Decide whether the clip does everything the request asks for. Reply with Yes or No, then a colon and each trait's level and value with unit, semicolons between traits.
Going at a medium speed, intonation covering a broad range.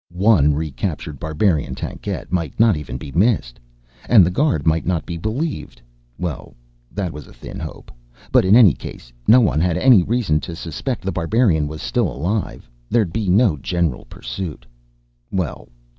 Yes: average, 165 wpm; wide, 5.8 semitones